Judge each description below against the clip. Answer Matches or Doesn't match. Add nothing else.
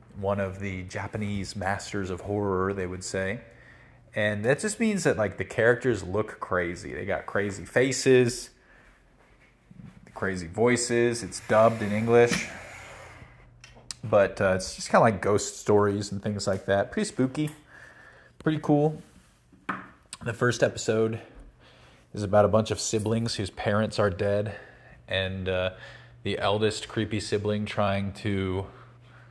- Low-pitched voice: Matches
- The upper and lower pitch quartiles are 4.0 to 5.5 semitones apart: Doesn't match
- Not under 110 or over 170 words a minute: Matches